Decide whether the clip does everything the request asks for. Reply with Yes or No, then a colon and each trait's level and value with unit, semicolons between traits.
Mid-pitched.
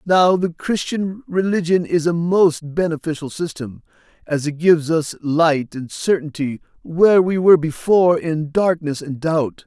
Yes: medium, 165 Hz